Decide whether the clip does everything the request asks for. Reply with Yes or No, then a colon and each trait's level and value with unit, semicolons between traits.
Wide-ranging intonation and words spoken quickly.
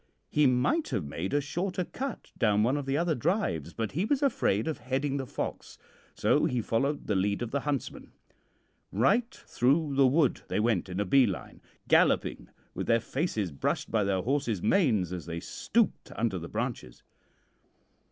No: wide, 6.3 semitones; average, 180 wpm